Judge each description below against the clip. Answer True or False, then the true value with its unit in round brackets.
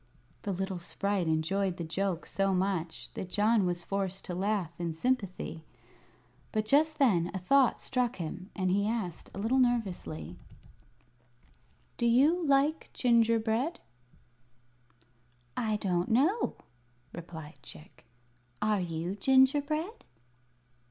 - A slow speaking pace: True (120 wpm)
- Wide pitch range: True (5.8 semitones)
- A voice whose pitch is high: True (200 Hz)